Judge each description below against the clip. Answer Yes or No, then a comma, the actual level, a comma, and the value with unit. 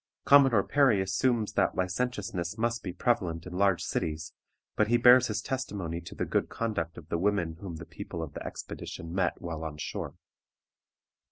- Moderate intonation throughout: No, wide, 5.7 semitones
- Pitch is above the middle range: No, very low, 95 Hz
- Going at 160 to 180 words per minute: Yes, average, 175 wpm